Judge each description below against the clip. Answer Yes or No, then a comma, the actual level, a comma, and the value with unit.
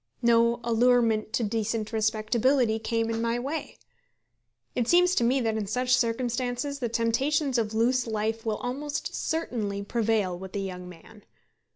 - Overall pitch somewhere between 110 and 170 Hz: No, high, 230 Hz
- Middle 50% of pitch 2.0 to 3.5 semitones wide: Yes, narrow, 2.4 semitones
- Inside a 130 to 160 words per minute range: Yes, average, 155 wpm